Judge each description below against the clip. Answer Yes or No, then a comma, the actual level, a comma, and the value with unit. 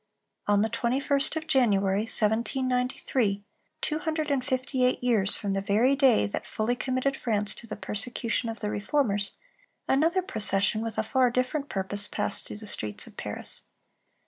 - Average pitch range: Yes, average, 4.4 semitones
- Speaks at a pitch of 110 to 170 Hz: No, high, 235 Hz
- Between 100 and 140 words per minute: No, average, 165 wpm